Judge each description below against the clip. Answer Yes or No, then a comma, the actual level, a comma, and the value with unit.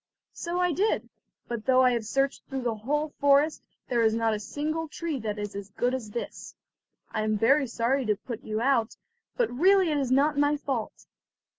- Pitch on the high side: Yes, very high, 260 Hz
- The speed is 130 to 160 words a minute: No, average, 200 wpm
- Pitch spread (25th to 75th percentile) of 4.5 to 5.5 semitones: Yes, average, 4.8 semitones